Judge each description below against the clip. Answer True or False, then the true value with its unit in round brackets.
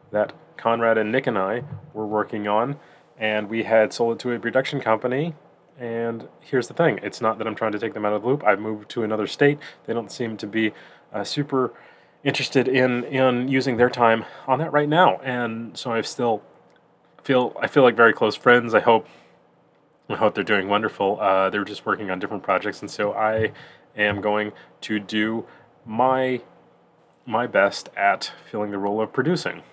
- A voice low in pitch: True (115 Hz)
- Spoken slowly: False (200 wpm)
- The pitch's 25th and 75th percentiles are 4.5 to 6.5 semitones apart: False (3.2 semitones)